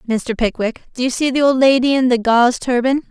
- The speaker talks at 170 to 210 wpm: No, fast, 230 wpm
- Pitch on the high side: Yes, very high, 250 Hz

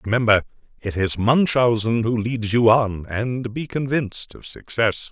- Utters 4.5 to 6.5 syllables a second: No, 4.3 syllables/s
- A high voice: No, low, 115 Hz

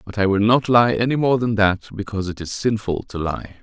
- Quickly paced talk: Yes, fast, 250 wpm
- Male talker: Yes, male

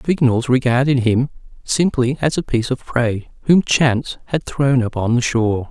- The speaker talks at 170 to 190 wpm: Yes, average, 180 wpm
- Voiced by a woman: No, male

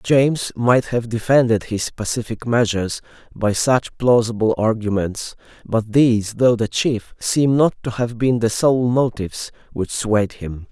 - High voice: No, low, 115 Hz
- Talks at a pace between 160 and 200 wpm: No, average, 150 wpm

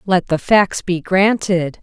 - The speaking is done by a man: No, female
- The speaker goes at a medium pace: Yes, average, 165 wpm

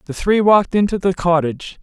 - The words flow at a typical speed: Yes, average, 195 wpm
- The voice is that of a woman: No, male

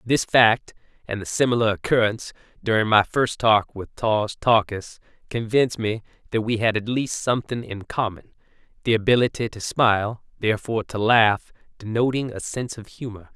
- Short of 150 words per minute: No, average, 155 wpm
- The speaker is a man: Yes, male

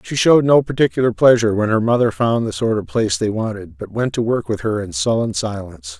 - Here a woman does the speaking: No, male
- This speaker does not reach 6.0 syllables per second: No, 6.1 syllables/s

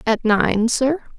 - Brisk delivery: No, average, 150 wpm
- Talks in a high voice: Yes, high, 240 Hz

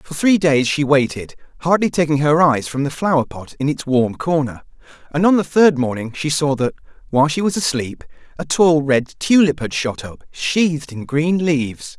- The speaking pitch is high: No, medium, 150 Hz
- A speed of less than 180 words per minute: No, average, 200 wpm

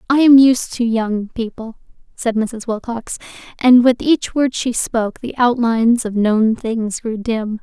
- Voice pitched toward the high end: Yes, high, 230 Hz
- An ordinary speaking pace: Yes, average, 175 wpm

